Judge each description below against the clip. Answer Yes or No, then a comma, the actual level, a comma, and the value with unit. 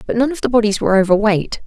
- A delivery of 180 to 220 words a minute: No, fast, 250 wpm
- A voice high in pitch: Yes, high, 215 Hz